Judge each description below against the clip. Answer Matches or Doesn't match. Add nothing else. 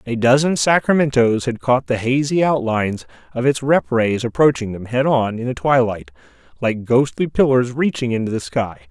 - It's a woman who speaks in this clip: Doesn't match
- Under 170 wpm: Doesn't match